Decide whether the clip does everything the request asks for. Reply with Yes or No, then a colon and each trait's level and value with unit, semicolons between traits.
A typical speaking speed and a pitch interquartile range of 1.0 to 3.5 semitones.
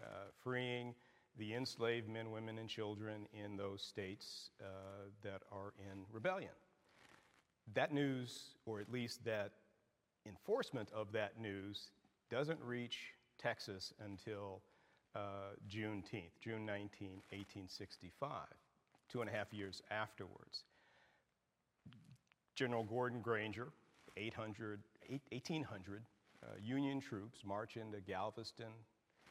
No: slow, 105 wpm; average, 2.8 semitones